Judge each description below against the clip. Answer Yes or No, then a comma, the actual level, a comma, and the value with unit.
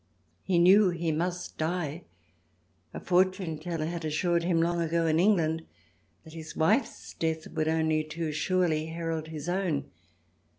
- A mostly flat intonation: Yes, narrow, 1.9 semitones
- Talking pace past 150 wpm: No, average, 145 wpm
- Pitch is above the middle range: No, medium, 165 Hz